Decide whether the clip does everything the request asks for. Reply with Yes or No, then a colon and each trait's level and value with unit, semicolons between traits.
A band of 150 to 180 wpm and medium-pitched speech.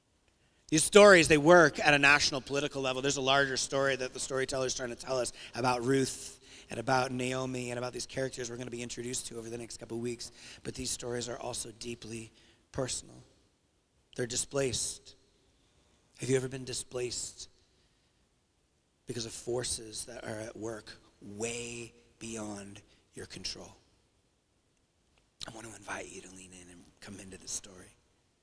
No: average, 170 wpm; low, 120 Hz